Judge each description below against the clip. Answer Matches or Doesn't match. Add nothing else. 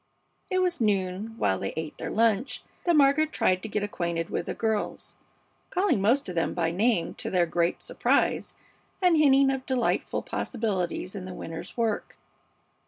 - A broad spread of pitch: Matches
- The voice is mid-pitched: Doesn't match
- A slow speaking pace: Doesn't match